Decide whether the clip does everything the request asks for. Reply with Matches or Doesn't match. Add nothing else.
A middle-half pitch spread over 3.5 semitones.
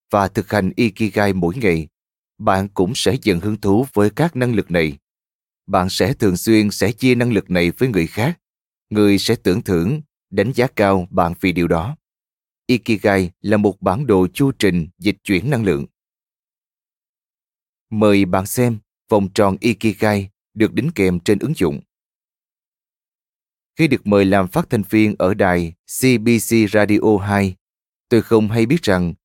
Doesn't match